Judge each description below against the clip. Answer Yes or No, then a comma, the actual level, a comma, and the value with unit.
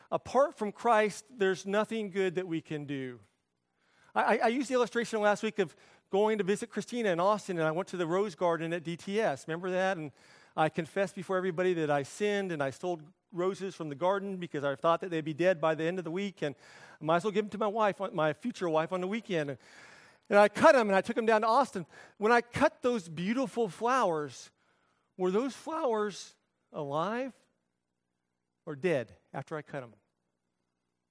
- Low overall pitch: No, medium, 185 Hz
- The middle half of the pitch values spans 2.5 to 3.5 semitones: No, wide, 5.6 semitones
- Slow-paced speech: No, fast, 205 wpm